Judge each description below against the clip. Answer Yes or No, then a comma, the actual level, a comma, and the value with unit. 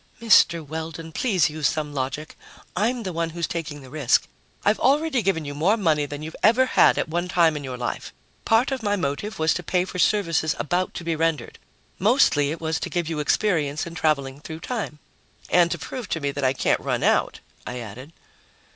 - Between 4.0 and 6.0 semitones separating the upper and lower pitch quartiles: Yes, average, 4.5 semitones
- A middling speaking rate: No, fast, 210 wpm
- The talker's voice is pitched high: No, medium, 165 Hz